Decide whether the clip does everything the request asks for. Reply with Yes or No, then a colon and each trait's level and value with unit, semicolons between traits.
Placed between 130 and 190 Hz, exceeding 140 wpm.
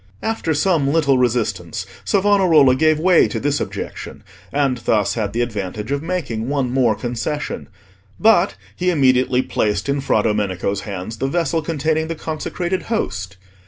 Yes: low, 135 Hz; average, 150 wpm